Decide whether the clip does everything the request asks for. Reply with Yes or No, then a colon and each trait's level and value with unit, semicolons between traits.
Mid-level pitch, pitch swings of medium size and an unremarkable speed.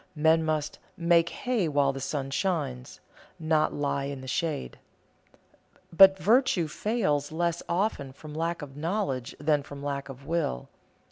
Yes: medium, 155 Hz; average, 3.5 semitones; average, 145 wpm